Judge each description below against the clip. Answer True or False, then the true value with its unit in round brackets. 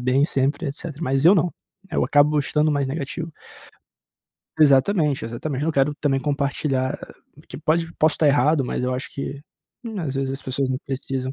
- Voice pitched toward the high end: False (140 Hz)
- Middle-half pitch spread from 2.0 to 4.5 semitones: True (2.4 semitones)